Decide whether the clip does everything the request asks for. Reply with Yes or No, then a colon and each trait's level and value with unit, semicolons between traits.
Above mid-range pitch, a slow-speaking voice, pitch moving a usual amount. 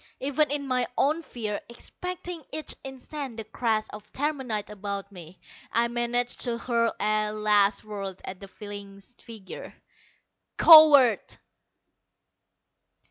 Yes: high, 230 Hz; slow, 120 wpm; average, 4.5 semitones